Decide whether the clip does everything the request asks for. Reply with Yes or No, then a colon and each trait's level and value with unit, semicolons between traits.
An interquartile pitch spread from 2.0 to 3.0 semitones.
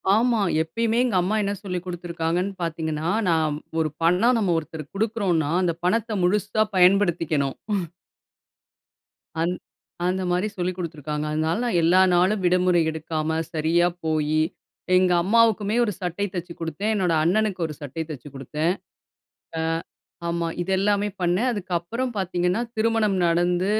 No: average, 3.8 semitones